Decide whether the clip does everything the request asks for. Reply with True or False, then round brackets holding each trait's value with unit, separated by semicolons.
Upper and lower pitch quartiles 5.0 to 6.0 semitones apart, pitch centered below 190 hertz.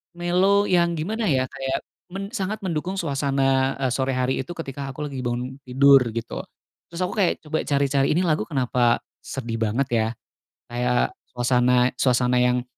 True (5.4 semitones; 135 Hz)